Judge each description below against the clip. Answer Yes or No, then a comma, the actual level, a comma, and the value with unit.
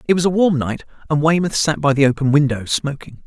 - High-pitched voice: No, medium, 145 Hz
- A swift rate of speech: Yes, fast, 240 wpm